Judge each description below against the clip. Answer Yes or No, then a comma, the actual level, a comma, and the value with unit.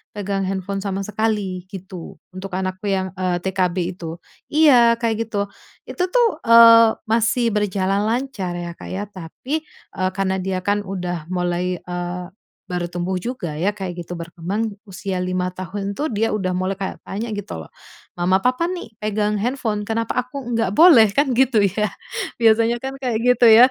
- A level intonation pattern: No, average, 3.7 semitones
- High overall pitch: Yes, high, 200 Hz